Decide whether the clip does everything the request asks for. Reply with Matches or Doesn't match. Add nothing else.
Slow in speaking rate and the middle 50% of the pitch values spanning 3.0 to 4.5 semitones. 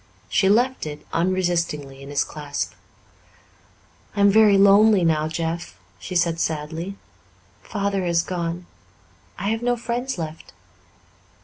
Matches